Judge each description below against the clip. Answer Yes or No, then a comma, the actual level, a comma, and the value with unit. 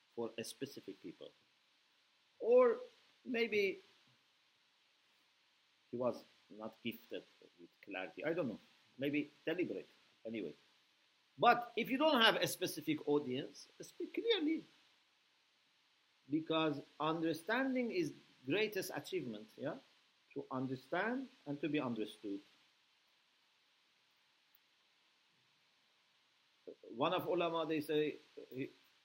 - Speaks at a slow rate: Yes, slow, 95 wpm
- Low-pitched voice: No, medium, 170 Hz